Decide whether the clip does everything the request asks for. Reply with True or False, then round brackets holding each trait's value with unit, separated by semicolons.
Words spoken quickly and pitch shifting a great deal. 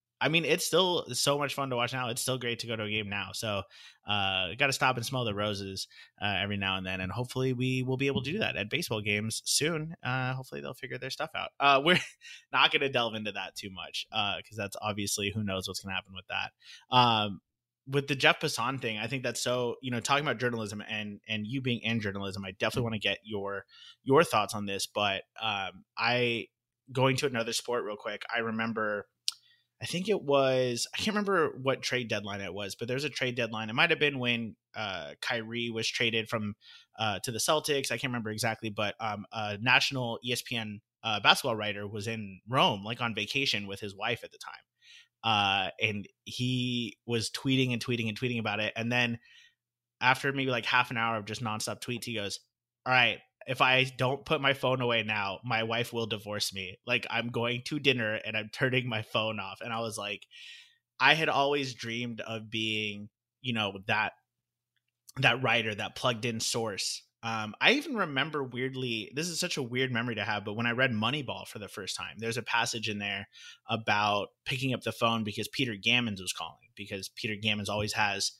False (215 wpm; 3.3 semitones)